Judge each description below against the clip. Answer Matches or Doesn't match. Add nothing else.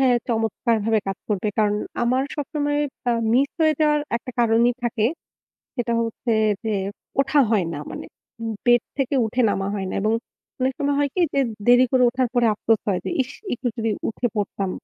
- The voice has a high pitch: Matches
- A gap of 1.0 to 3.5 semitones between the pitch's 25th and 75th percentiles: Matches